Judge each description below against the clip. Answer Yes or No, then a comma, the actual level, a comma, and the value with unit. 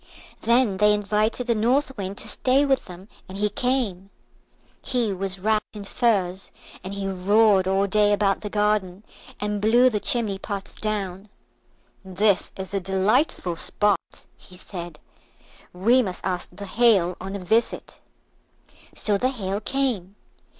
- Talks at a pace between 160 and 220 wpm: No, average, 150 wpm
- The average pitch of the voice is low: No, high, 205 Hz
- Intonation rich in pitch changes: No, narrow, 2.6 semitones